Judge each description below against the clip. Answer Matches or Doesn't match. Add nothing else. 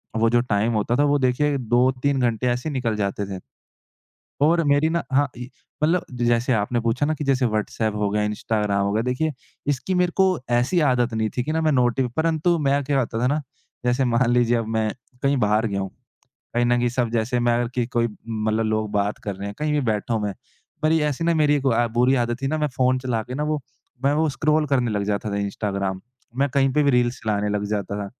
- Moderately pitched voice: Doesn't match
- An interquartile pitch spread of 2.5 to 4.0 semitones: Doesn't match